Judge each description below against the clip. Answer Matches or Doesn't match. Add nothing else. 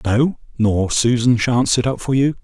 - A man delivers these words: Matches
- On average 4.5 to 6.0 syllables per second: Doesn't match